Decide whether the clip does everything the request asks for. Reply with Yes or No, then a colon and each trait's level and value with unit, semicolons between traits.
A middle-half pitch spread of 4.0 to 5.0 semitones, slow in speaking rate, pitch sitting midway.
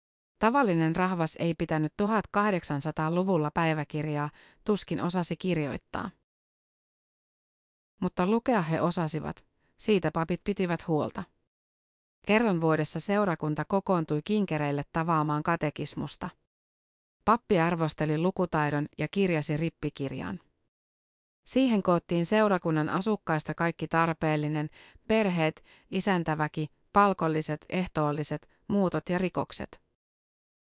No: average, 3.6 semitones; slow, 85 wpm; medium, 165 Hz